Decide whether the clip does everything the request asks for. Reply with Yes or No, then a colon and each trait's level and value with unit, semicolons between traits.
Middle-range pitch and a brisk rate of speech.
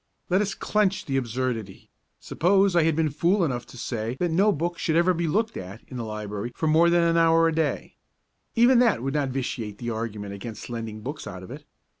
Yes: medium, 150 Hz; fast, 220 wpm